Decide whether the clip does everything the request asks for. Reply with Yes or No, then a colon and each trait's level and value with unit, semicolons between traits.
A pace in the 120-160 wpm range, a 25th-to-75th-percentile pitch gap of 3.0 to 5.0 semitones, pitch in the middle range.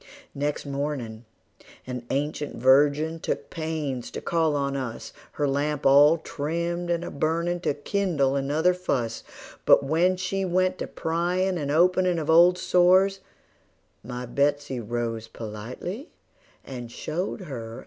Yes: average, 145 wpm; average, 4.5 semitones; medium, 150 Hz